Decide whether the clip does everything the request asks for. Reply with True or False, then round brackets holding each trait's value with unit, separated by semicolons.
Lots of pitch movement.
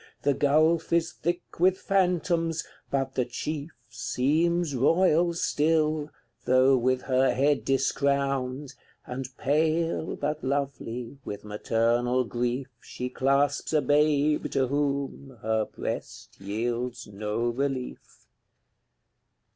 False (3.7 semitones)